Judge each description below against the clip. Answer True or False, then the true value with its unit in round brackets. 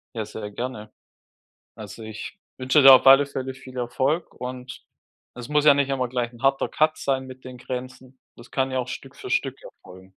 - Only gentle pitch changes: True (1.9 semitones)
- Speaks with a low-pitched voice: True (130 Hz)